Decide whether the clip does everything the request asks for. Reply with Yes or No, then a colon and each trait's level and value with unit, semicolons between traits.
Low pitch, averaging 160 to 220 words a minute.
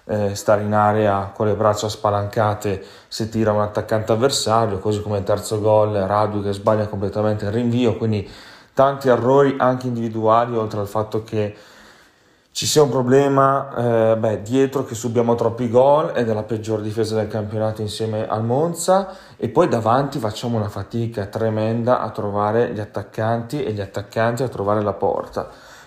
Yes: low, 110 Hz; average, 165 wpm